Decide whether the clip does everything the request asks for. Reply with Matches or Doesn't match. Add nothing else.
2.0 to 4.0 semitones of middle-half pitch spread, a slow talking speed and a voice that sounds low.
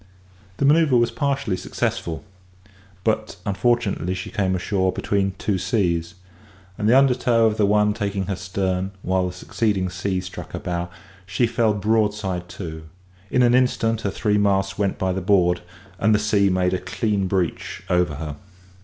Doesn't match